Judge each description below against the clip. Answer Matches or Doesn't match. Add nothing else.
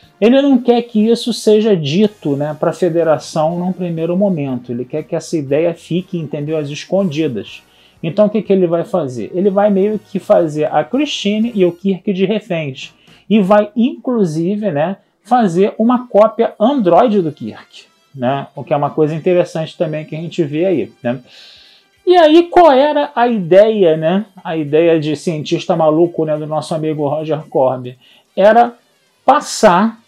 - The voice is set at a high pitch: Doesn't match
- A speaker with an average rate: Matches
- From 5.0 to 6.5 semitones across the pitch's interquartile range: Matches